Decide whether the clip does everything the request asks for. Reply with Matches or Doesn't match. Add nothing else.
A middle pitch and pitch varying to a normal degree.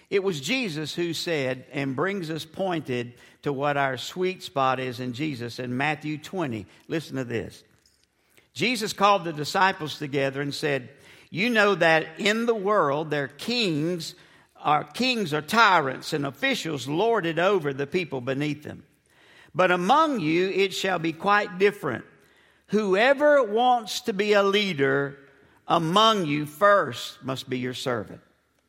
Doesn't match